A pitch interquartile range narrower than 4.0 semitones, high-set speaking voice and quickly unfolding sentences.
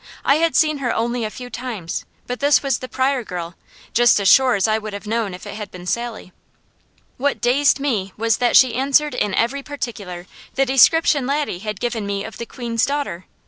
No: average, 4.6 semitones; high, 240 Hz; fast, 210 wpm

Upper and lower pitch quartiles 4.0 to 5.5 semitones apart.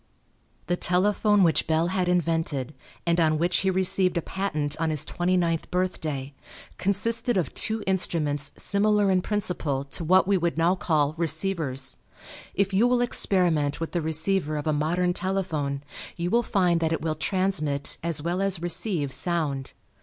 No: average, 3.6 semitones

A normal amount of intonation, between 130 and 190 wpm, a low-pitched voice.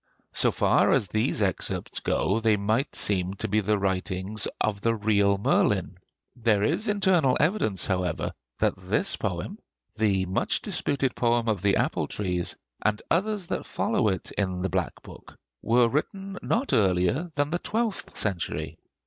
No: wide, 6.7 semitones; average, 155 wpm; low, 110 Hz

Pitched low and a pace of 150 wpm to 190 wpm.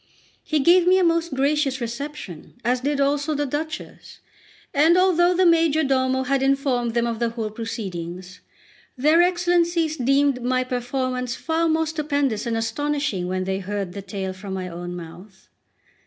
No: very high, 265 Hz; average, 155 wpm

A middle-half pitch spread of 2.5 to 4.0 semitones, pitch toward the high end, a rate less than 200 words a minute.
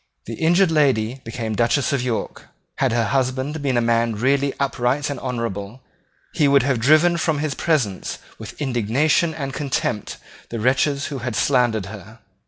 No: average, 3.6 semitones; low, 130 Hz; average, 165 wpm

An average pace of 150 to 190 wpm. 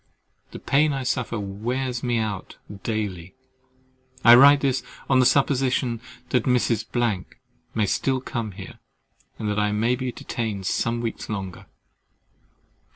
No: average, 140 wpm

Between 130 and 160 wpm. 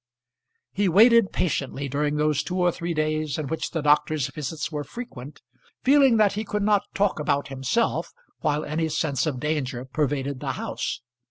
No: average, 170 wpm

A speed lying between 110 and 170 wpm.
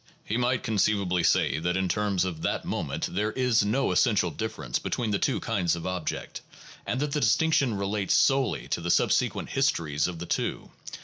No: average, 180 wpm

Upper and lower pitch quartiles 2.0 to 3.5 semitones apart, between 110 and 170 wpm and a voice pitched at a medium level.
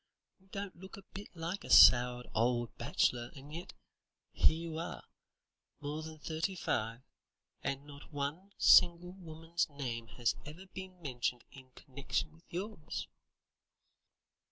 No: average, 5.1 semitones; slow, 135 wpm; medium, 155 Hz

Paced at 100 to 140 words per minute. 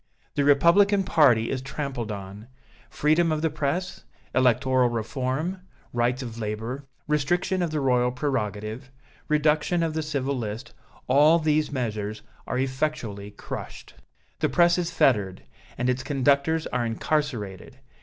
Yes: slow, 135 wpm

